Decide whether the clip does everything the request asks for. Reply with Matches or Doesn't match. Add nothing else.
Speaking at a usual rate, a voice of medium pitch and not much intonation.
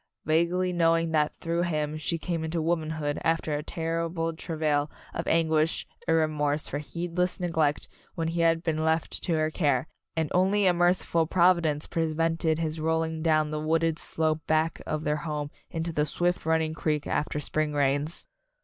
Matches